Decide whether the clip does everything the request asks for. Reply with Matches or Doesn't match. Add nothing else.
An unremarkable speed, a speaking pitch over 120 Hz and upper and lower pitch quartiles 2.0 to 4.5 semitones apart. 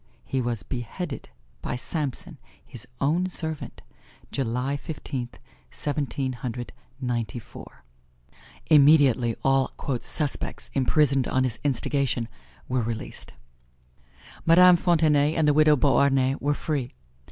Doesn't match